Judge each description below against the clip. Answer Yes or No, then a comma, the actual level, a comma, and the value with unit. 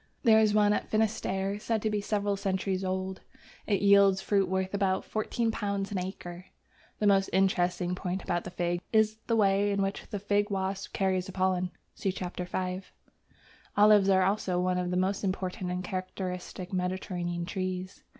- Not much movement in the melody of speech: Yes, narrow, 1.8 semitones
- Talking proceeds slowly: No, average, 170 wpm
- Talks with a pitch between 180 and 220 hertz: Yes, high, 190 Hz